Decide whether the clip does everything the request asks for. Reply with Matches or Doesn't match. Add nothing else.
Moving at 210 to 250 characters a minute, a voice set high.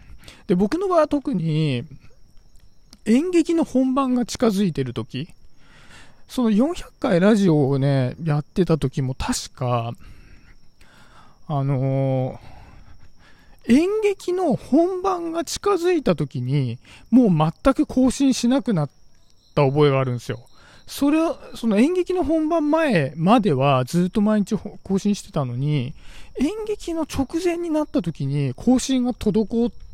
Matches